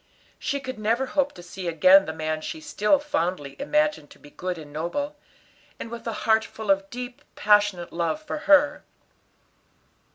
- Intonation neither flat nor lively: No, wide, 8.5 semitones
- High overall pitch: Yes, high, 215 Hz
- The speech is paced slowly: No, average, 170 wpm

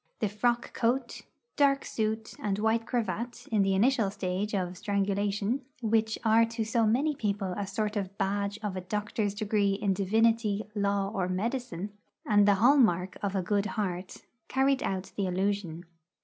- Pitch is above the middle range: Yes, high, 205 Hz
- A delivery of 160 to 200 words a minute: Yes, average, 165 wpm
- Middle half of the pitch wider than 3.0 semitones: No, narrow, 2.5 semitones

